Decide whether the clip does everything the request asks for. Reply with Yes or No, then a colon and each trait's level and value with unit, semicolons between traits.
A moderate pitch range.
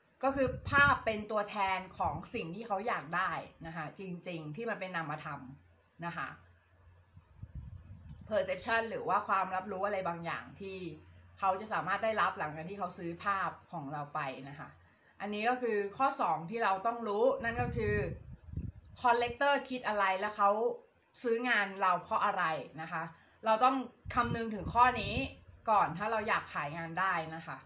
No: wide, 6.3 semitones